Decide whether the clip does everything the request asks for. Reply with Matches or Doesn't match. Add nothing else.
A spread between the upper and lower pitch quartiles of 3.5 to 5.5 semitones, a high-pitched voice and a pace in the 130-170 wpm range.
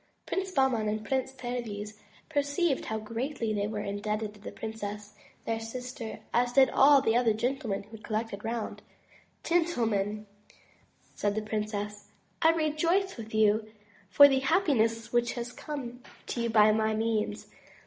Matches